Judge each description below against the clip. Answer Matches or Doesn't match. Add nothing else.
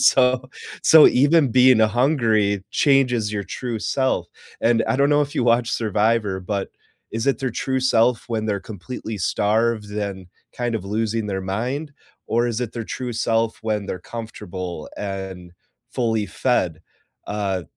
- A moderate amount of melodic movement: Matches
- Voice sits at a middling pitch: Doesn't match